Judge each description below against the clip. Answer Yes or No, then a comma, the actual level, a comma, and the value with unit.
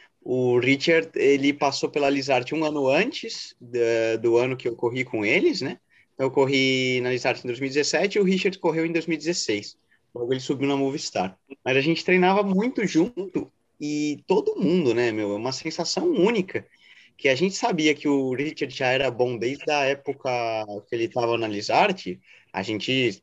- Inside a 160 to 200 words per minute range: Yes, average, 180 wpm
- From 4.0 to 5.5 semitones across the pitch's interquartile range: Yes, average, 4.7 semitones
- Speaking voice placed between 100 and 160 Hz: Yes, low, 135 Hz